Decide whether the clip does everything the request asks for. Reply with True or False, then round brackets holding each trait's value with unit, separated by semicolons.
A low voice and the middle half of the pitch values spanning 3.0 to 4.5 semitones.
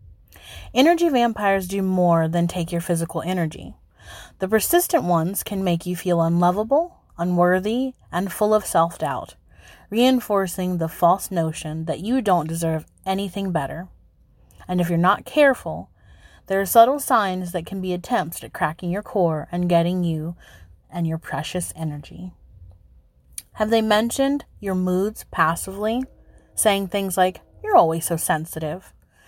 False (180 Hz; 3.9 semitones)